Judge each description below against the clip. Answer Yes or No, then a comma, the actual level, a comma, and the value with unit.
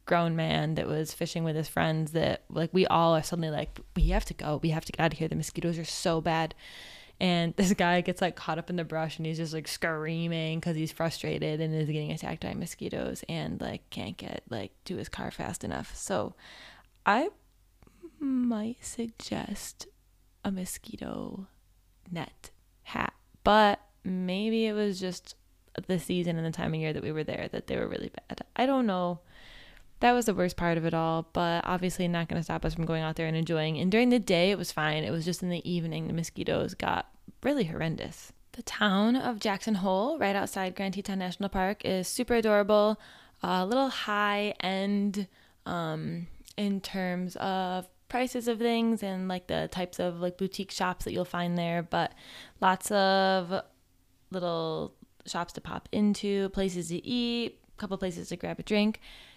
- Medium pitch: Yes, medium, 180 Hz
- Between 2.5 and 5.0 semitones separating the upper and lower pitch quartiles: Yes, average, 3.7 semitones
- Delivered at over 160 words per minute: Yes, average, 195 wpm